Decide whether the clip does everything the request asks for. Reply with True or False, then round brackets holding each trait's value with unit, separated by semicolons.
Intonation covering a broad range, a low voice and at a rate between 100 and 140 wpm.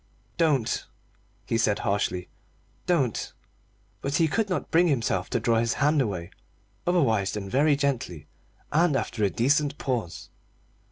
True (6.1 semitones; 130 Hz; 135 wpm)